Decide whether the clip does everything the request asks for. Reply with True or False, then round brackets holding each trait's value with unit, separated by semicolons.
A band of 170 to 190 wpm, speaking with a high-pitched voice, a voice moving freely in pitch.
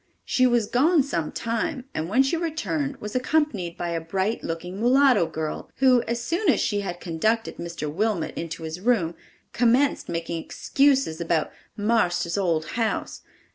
False (160 wpm; 215 Hz; 7.4 semitones)